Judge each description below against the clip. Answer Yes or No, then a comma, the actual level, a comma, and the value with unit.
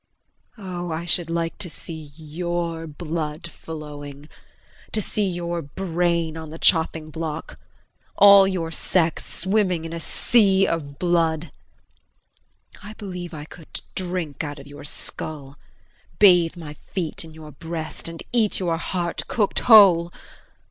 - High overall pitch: No, medium, 165 Hz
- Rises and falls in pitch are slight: Yes, narrow, 2.3 semitones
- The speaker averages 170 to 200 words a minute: No, slow, 135 wpm